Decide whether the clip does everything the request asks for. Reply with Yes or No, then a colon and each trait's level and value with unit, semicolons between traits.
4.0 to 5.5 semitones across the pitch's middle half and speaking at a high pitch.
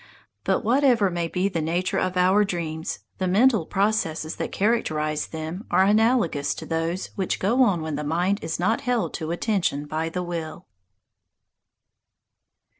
No: average, 4.3 semitones; medium, 180 Hz